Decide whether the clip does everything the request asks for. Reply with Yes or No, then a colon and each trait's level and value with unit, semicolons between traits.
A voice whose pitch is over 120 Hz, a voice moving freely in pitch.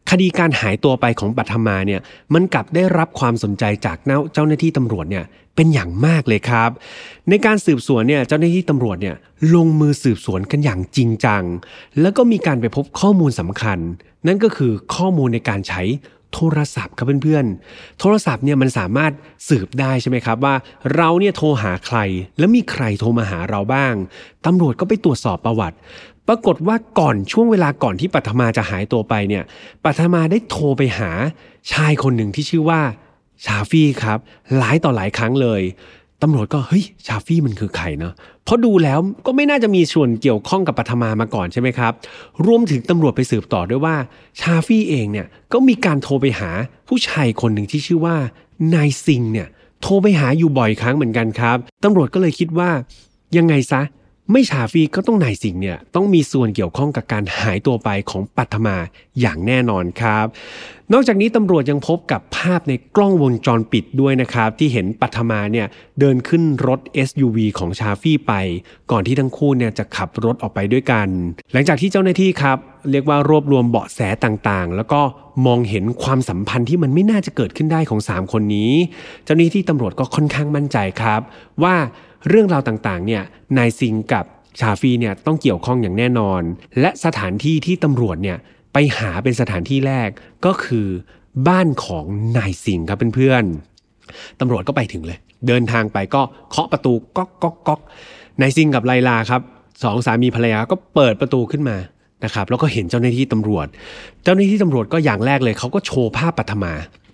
Yes: low, 130 Hz; wide, 6.2 semitones